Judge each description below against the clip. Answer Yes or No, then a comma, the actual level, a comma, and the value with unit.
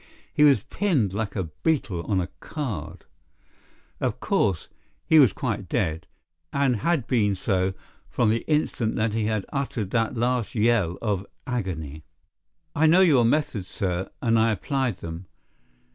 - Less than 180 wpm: Yes, average, 150 wpm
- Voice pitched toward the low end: Yes, low, 110 Hz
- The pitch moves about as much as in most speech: No, wide, 5.7 semitones